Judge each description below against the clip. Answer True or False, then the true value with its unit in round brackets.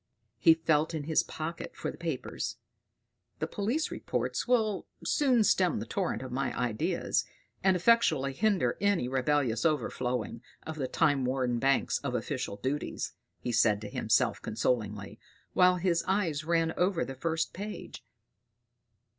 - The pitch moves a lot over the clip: True (6.2 semitones)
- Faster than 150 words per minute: False (145 wpm)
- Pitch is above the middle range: False (155 Hz)